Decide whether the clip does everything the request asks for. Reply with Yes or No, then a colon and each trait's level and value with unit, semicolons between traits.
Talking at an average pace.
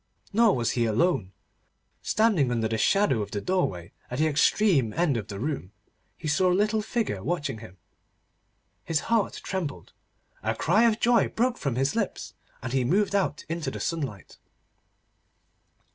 Yes: average, 160 wpm